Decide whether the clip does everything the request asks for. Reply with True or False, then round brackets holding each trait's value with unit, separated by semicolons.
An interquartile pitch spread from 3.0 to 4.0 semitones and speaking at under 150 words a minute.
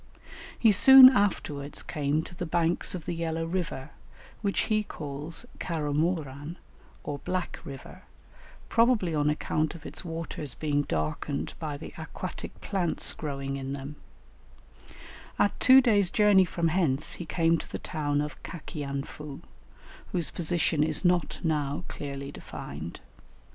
True (3.6 semitones; 135 wpm)